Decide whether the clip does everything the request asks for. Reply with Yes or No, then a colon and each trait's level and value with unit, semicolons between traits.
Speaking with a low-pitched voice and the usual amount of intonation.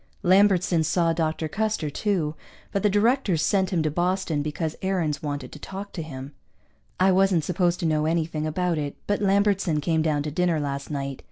No: medium, 165 Hz; average, 3.9 semitones